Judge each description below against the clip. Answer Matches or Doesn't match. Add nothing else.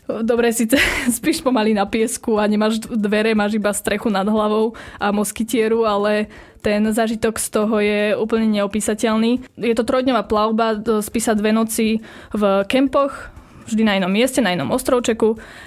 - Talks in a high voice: Matches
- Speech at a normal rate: Matches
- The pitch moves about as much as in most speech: Doesn't match